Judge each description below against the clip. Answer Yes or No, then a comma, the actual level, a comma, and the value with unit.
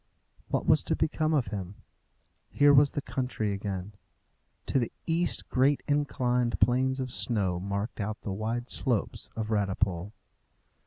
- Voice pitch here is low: Yes, low, 120 Hz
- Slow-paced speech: No, average, 145 wpm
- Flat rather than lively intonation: No, average, 4.7 semitones